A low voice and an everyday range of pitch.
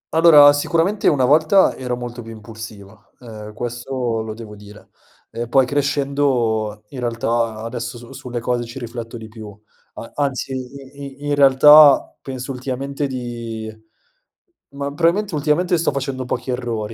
Yes: low, 125 Hz; average, 3.7 semitones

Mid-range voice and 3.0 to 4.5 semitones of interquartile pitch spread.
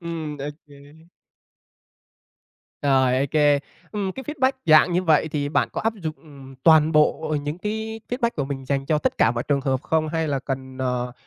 Yes: medium, 150 Hz; average, 3.3 semitones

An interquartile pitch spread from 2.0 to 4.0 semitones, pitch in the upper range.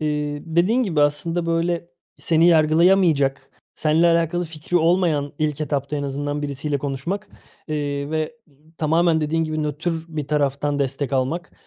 No: narrow, 2.5 semitones; medium, 155 Hz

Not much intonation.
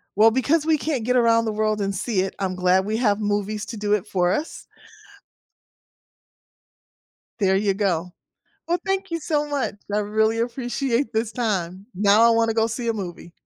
No: average, 3.4 semitones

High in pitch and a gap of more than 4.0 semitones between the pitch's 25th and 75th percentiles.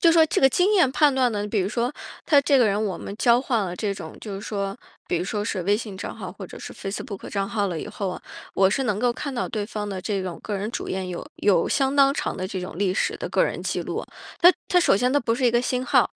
Yes: high, 210 Hz; average, 4.6 semitones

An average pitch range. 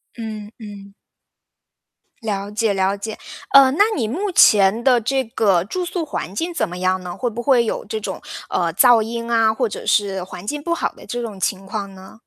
Yes: average, 3.7 semitones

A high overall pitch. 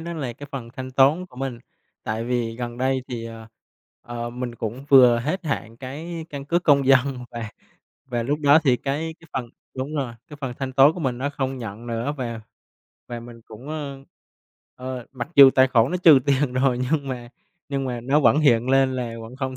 No: low, 130 Hz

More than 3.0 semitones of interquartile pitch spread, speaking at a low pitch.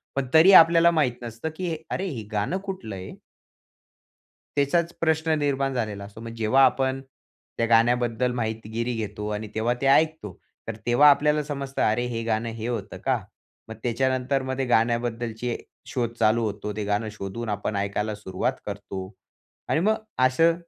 Yes: average, 4.2 semitones; low, 120 Hz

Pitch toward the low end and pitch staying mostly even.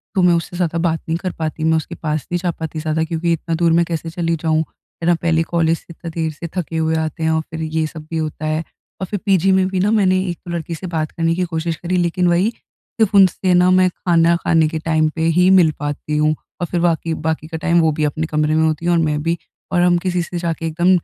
No: medium, 165 Hz; narrow, 1.7 semitones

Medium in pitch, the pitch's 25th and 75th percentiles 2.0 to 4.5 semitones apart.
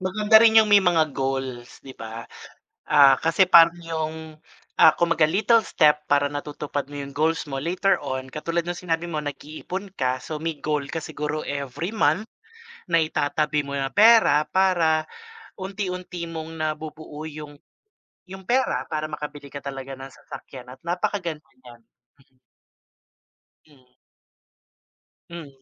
Yes: medium, 155 Hz; average, 3.4 semitones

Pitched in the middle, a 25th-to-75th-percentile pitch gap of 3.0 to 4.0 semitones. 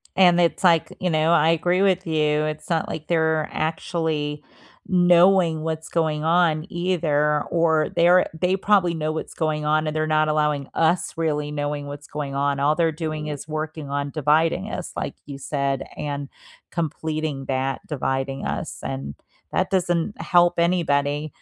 No: medium, 155 Hz; narrow, 2.4 semitones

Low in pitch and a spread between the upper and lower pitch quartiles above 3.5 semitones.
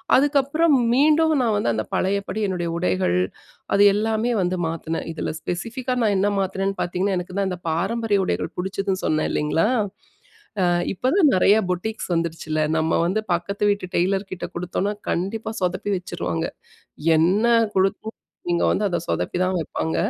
No: high, 190 Hz; average, 3.9 semitones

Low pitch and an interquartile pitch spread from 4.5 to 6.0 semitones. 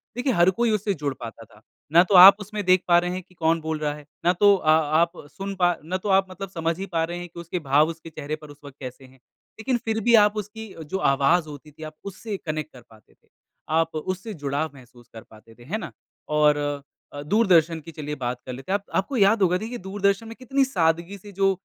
No: medium, 170 Hz; average, 4.9 semitones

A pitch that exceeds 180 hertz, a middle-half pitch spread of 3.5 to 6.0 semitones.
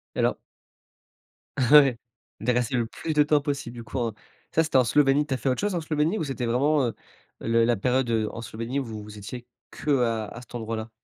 No: low, 125 Hz; average, 4.1 semitones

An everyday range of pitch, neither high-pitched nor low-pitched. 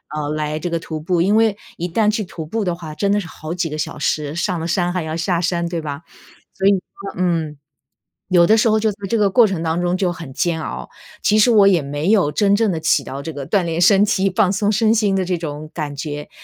Yes: average, 4.1 semitones; medium, 175 Hz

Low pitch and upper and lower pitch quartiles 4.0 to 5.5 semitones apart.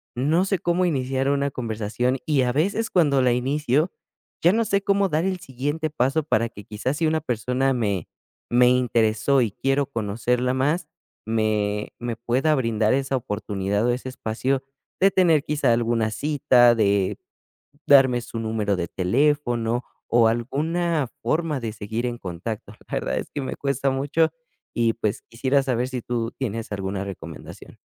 Yes: low, 125 Hz; average, 4.3 semitones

